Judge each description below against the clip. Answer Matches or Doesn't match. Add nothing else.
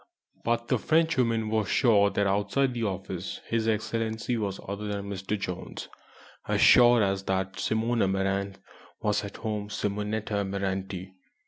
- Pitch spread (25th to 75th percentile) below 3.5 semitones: Matches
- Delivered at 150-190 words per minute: Doesn't match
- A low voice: Matches